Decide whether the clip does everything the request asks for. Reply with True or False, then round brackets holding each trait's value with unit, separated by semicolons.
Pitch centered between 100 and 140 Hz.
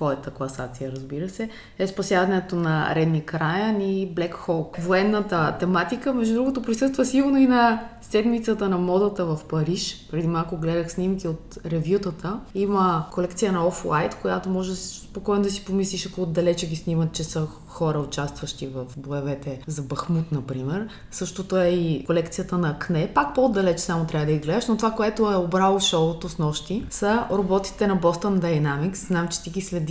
False (180 Hz)